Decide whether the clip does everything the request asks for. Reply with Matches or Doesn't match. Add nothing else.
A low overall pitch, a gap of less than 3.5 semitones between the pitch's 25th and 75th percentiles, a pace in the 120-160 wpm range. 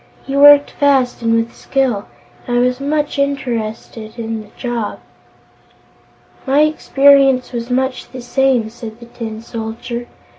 Doesn't match